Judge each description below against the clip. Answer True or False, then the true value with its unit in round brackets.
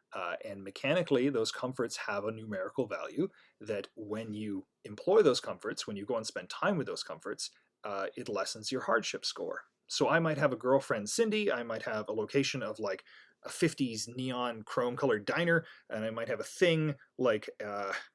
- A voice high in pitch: False (135 Hz)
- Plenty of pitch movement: True (7.4 semitones)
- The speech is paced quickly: False (190 wpm)